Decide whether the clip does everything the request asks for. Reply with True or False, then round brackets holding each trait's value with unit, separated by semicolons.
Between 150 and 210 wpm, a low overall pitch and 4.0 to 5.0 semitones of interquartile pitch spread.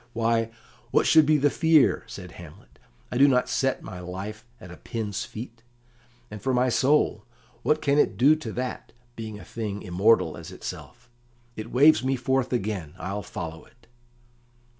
True (170 wpm; 115 Hz; 4.4 semitones)